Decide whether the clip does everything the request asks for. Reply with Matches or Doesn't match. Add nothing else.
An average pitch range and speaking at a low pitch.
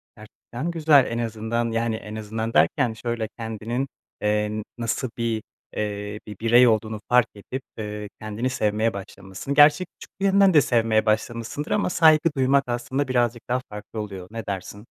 Matches